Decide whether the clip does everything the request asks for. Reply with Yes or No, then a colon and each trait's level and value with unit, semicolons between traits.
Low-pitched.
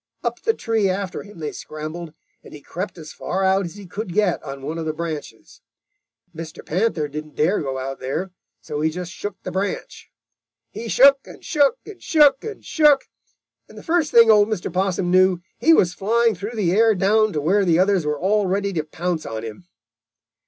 No: medium, 185 Hz